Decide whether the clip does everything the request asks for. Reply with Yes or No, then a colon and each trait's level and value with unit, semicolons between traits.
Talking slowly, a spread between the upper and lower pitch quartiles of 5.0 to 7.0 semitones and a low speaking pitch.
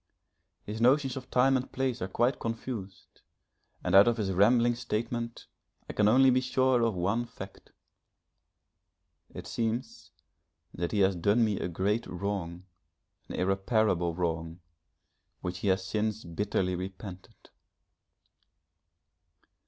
No: slow, 130 wpm; average, 4.2 semitones; low, 105 Hz